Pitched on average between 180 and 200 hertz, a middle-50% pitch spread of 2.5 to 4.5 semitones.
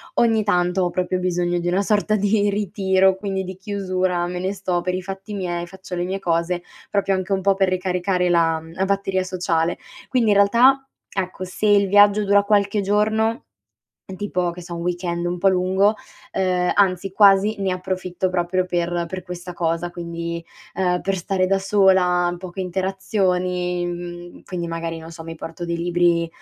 No: medium, 185 Hz; narrow, 1.9 semitones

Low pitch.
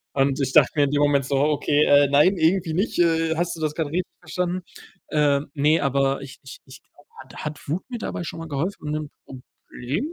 No: medium, 150 Hz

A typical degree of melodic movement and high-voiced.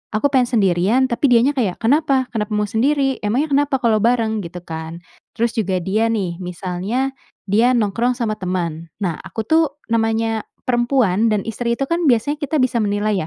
Yes: average, 4.5 semitones; high, 225 Hz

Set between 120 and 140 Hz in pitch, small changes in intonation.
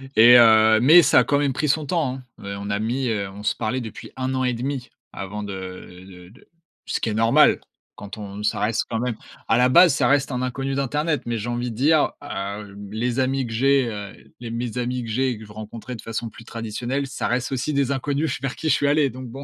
No: low, 125 Hz; average, 3.7 semitones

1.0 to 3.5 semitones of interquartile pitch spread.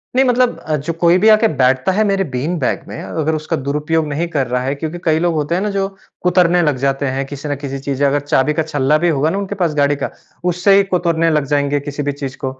No: average, 4.0 semitones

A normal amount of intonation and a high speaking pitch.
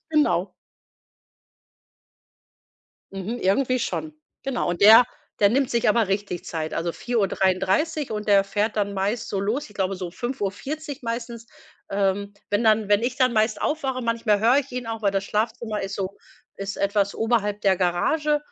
Yes: average, 3.7 semitones; high, 210 Hz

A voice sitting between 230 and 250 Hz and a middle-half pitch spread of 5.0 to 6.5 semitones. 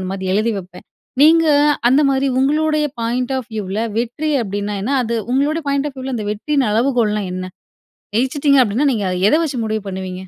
Yes: high, 240 Hz; average, 5.3 semitones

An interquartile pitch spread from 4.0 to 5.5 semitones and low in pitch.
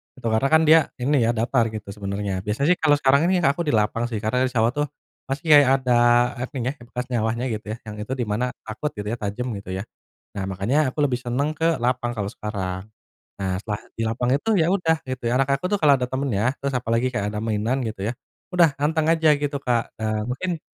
Yes: average, 4.7 semitones; low, 125 Hz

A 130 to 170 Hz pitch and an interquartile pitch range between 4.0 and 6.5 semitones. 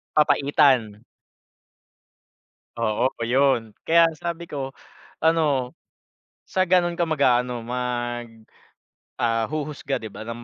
Yes: low, 135 Hz; average, 4.4 semitones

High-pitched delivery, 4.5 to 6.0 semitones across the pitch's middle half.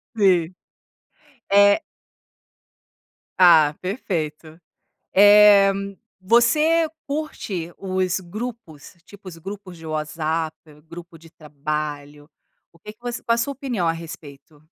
No: medium, 180 Hz; average, 4.8 semitones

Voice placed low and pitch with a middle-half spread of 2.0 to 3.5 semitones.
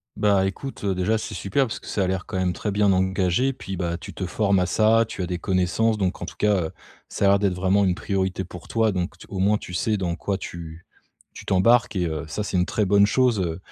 Yes: very low, 95 Hz; narrow, 2.5 semitones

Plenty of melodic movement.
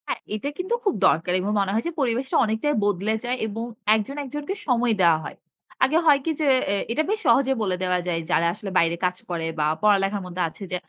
Yes: wide, 6.6 semitones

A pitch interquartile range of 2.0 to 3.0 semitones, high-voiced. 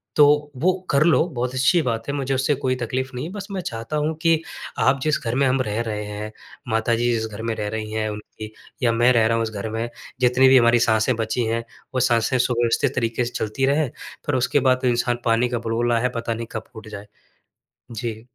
No: average, 2.7 semitones; low, 120 Hz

